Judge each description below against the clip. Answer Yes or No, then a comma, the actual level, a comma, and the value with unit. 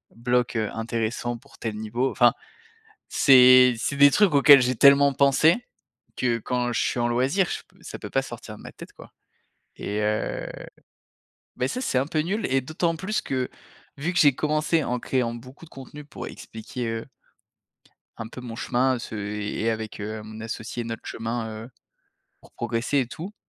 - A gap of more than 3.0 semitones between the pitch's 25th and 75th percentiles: Yes, average, 3.6 semitones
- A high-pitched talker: No, low, 125 Hz